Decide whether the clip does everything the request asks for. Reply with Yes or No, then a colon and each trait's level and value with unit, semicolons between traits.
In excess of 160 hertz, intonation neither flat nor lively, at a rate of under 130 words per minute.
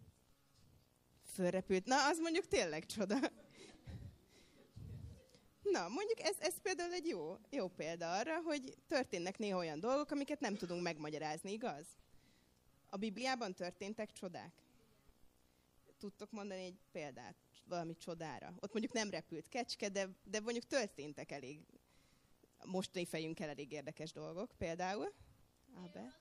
No: high, 190 Hz; wide, 8.3 semitones; average, 120 wpm